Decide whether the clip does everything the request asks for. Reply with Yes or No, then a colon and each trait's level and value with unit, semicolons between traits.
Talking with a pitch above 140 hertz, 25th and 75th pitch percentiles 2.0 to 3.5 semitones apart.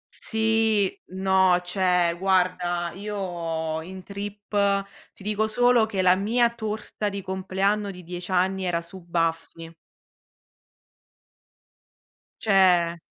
Yes: high, 190 Hz; narrow, 2.6 semitones